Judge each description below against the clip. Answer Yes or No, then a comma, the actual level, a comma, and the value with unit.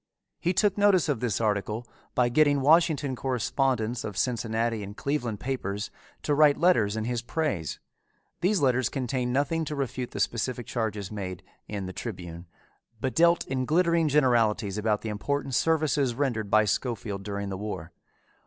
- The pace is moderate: Yes, average, 160 wpm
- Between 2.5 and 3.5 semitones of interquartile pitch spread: No, average, 5.2 semitones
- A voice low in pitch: Yes, low, 120 Hz